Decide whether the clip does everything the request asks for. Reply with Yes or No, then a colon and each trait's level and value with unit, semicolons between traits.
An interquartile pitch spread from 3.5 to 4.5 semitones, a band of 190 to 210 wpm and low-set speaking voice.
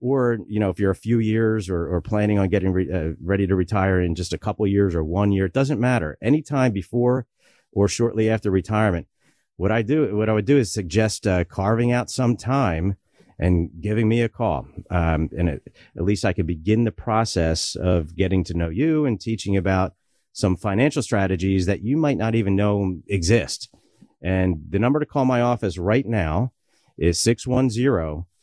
Yes: average, 4.1 semitones; average, 200 wpm; low, 105 Hz